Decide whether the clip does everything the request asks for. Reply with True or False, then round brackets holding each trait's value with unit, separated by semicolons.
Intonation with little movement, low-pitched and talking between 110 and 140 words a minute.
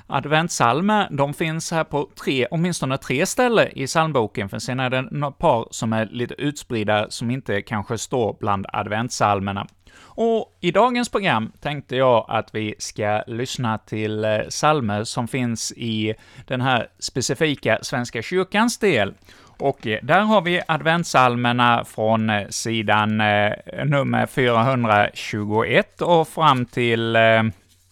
False (5.1 semitones; 120 Hz; 135 wpm)